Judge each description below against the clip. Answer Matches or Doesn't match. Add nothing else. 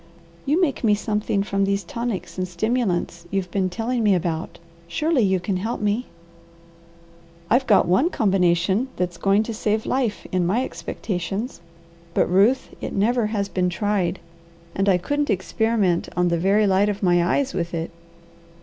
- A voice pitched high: Matches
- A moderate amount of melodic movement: Matches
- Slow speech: Doesn't match